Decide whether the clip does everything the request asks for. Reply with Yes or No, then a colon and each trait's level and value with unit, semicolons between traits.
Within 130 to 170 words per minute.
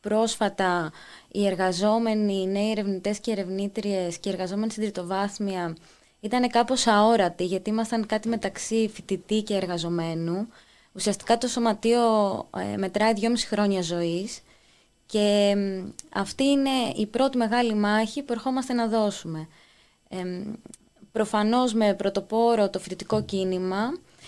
No: slow, 115 wpm